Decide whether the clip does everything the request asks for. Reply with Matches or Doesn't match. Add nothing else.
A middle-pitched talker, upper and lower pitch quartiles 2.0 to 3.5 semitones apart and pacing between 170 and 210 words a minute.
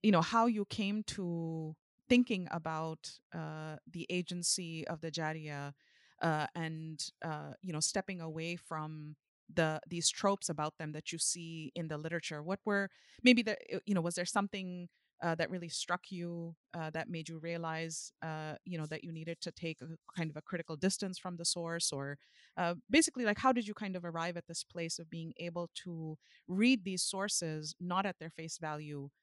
Matches